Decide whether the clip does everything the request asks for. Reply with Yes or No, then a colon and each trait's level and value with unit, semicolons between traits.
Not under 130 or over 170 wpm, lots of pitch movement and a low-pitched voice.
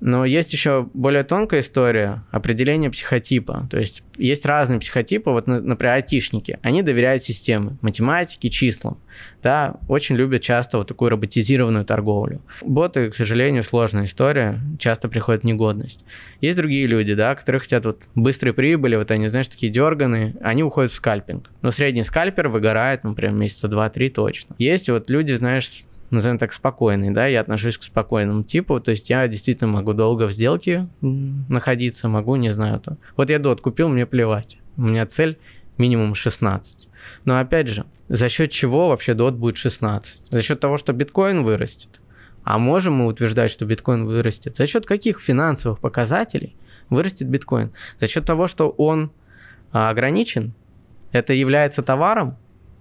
No: fast, 160 wpm; average, 3.7 semitones; low, 125 Hz